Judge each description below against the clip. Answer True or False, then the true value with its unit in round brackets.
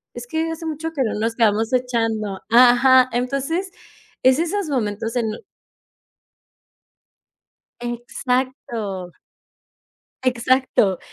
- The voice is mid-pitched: False (250 Hz)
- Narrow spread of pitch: False (3.1 semitones)